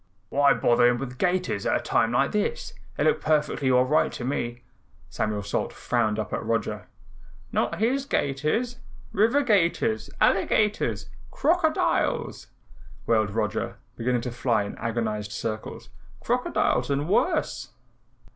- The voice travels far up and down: Yes, wide, 9.0 semitones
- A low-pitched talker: Yes, low, 130 Hz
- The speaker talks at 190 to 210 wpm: No, slow, 135 wpm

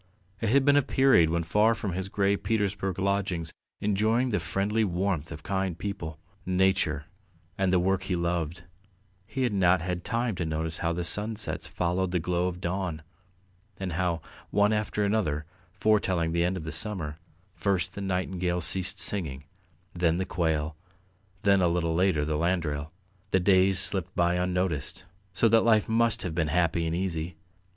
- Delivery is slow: No, average, 170 wpm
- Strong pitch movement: No, average, 3.0 semitones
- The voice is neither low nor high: No, very low, 90 Hz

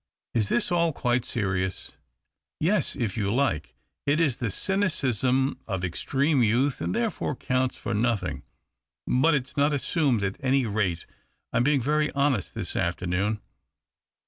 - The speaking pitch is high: No, low, 125 Hz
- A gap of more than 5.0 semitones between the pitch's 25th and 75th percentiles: Yes, wide, 5.6 semitones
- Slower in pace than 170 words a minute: Yes, average, 155 wpm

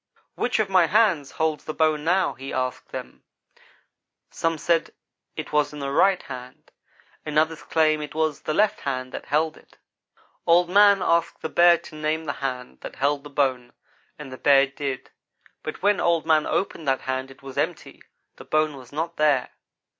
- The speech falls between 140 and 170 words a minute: No, average, 190 wpm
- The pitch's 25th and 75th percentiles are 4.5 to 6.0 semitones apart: No, average, 3.4 semitones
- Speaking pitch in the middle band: Yes, medium, 155 Hz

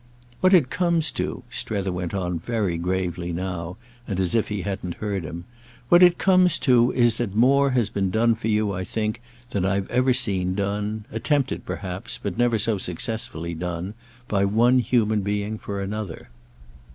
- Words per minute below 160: No, average, 165 wpm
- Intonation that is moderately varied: Yes, average, 4.3 semitones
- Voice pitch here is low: Yes, low, 105 Hz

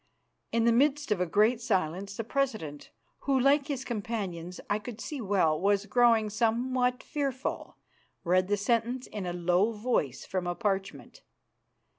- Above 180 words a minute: No, average, 155 wpm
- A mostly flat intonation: No, average, 4.7 semitones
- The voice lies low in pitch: No, high, 215 Hz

